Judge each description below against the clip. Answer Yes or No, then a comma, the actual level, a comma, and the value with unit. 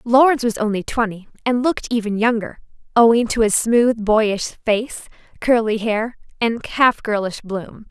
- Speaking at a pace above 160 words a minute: No, average, 150 wpm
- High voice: Yes, high, 225 Hz